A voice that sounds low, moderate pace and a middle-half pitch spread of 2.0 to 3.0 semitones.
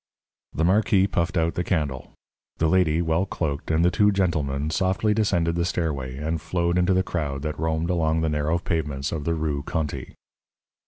Yes: very low, 80 Hz; average, 180 wpm; average, 2.7 semitones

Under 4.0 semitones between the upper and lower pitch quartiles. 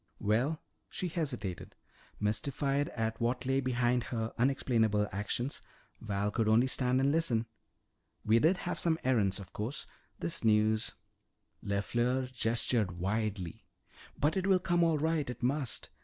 No: average, 4.5 semitones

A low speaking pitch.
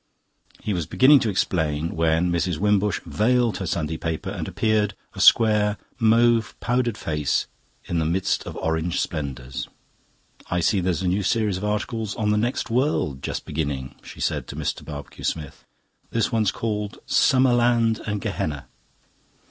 Yes: low, 100 Hz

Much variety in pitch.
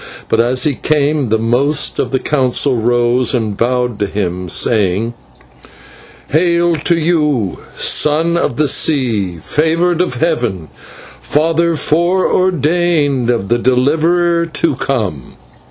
Yes: wide, 5.7 semitones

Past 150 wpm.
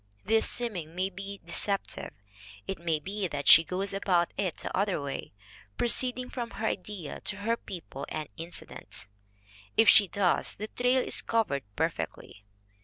Yes: average, 160 wpm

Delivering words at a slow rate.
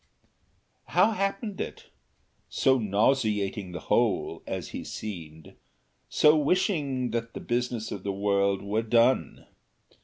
Yes: slow, 120 wpm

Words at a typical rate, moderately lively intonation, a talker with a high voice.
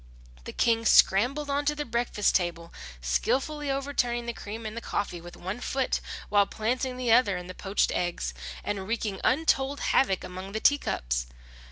No: average, 170 wpm; wide, 5.7 semitones; high, 225 Hz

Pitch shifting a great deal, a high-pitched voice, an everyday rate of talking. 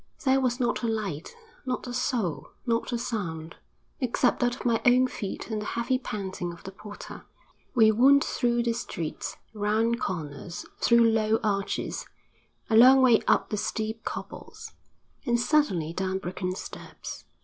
No: average, 4.0 semitones; high, 225 Hz; average, 160 wpm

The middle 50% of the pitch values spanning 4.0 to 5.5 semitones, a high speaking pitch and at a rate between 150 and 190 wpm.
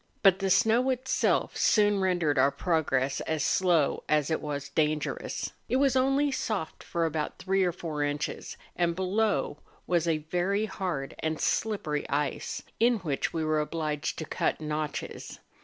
No: average, 4.6 semitones; medium, 165 Hz; average, 155 wpm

